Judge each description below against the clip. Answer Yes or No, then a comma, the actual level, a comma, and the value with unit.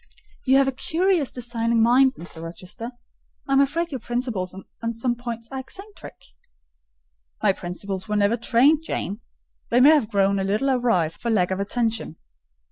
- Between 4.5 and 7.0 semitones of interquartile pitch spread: Yes, average, 5.0 semitones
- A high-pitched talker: Yes, high, 235 Hz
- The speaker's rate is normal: Yes, average, 165 wpm